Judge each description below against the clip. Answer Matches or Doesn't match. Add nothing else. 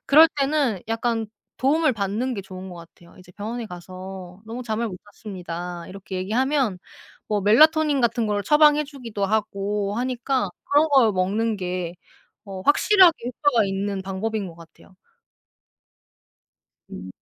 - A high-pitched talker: Matches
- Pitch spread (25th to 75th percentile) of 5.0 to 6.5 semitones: Matches